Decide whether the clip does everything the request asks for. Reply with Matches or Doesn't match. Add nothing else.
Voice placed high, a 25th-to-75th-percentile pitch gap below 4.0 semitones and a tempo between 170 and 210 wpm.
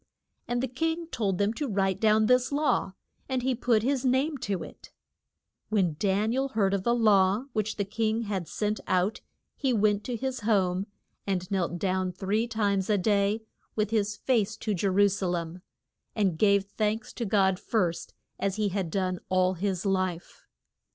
Matches